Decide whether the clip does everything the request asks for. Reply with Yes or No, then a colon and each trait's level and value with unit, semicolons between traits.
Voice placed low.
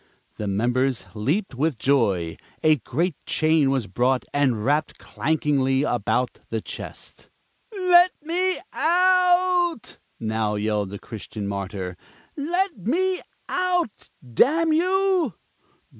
No: medium, 145 Hz